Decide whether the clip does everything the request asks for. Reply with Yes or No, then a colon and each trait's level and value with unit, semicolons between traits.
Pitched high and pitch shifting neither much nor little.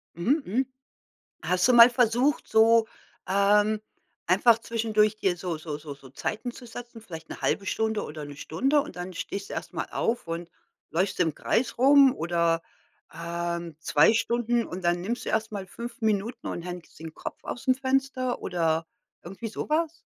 No: high, 210 Hz; wide, 5.7 semitones